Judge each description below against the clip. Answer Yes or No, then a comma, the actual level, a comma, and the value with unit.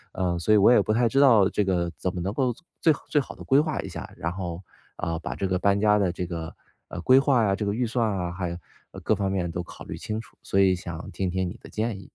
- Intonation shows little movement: No, average, 3.9 semitones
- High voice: No, very low, 95 Hz